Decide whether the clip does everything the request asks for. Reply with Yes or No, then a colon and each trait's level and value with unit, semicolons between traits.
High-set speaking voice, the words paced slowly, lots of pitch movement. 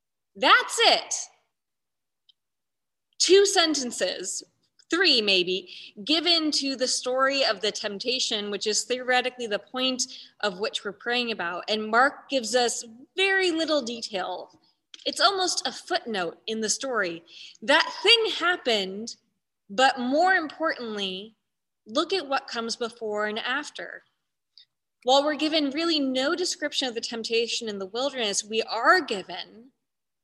Yes: very high, 250 Hz; slow, 130 wpm; wide, 6.0 semitones